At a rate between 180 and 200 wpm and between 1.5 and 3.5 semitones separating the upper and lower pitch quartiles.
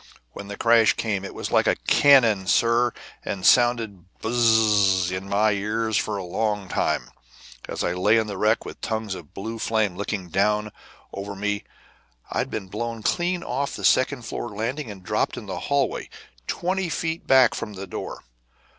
No: average, 170 wpm; average, 3.0 semitones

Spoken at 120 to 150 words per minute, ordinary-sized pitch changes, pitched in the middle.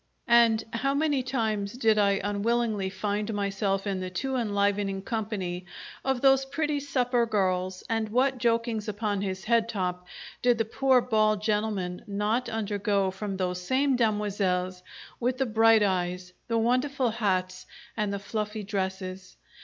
No: average, 145 wpm; average, 3.3 semitones; high, 210 Hz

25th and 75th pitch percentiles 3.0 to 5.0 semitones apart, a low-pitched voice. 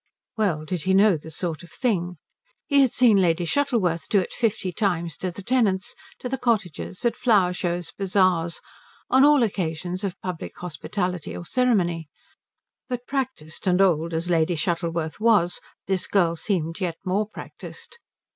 No: average, 4.3 semitones; medium, 185 Hz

